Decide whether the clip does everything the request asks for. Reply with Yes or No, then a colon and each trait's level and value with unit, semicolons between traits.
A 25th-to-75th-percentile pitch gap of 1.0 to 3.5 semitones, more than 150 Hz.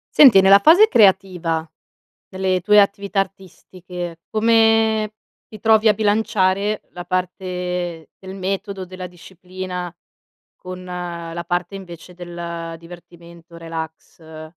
Yes: narrow, 2.5 semitones; medium, 185 Hz